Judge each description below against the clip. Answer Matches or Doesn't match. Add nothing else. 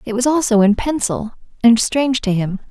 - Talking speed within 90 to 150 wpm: Doesn't match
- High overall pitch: Matches